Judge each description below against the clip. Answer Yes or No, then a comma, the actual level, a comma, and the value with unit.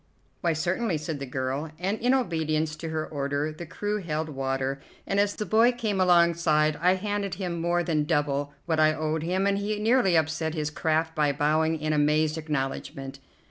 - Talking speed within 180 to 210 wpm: Yes, average, 185 wpm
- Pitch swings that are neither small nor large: Yes, average, 3.4 semitones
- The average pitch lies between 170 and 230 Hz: No, medium, 160 Hz